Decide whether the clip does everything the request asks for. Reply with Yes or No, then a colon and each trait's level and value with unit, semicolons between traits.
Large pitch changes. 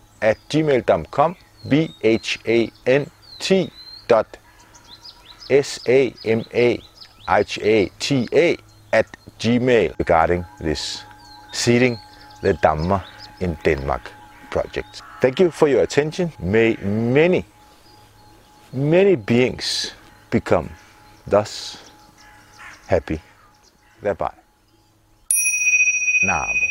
Yes: wide, 5.8 semitones